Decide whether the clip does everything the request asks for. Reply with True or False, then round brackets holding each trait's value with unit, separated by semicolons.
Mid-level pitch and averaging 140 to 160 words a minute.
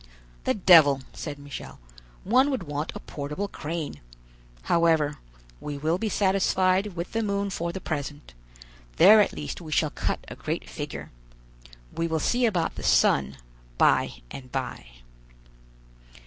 True (165 Hz; 145 wpm)